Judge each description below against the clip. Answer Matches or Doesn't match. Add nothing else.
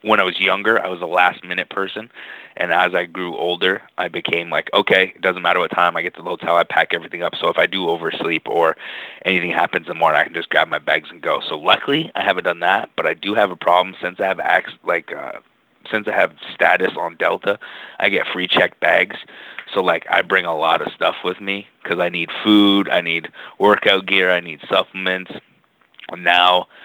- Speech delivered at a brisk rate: Matches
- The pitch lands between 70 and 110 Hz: Matches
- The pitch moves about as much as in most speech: Doesn't match